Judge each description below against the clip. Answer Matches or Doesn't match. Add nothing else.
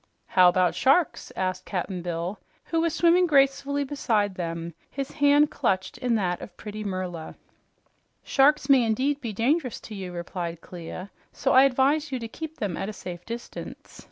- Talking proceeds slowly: Doesn't match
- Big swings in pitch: Matches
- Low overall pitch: Doesn't match